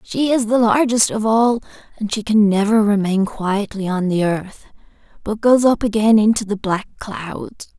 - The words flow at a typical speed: Yes, average, 175 wpm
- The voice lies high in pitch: Yes, high, 215 Hz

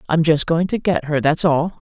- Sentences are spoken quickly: Yes, fast, 255 wpm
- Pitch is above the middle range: No, medium, 160 Hz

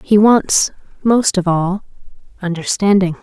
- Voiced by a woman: Yes, female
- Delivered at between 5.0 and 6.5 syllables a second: No, 4.0 syllables/s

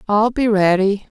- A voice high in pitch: Yes, high, 210 Hz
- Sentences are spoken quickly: No, average, 150 wpm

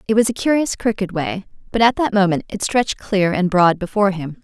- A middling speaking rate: No, fast, 230 wpm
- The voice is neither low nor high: No, high, 200 Hz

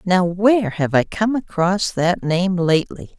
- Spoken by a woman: Yes, female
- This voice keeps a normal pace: Yes, average, 170 wpm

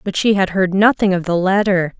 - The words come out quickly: Yes, fast, 240 wpm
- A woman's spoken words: Yes, female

